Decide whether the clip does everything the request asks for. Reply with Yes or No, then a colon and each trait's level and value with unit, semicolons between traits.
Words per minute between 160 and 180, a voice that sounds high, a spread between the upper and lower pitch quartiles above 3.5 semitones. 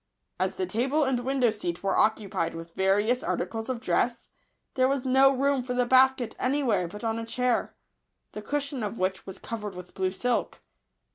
No: average, 190 wpm; high, 240 Hz; average, 4.2 semitones